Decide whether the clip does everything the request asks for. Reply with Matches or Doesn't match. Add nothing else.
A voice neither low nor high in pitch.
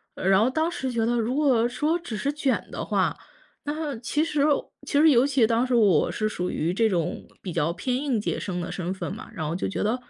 Doesn't match